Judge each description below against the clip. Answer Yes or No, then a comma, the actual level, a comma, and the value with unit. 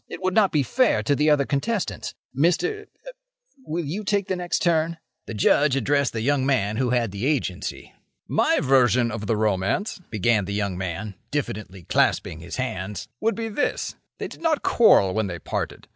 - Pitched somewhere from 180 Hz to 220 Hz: No, low, 135 Hz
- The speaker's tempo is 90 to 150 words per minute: No, average, 185 wpm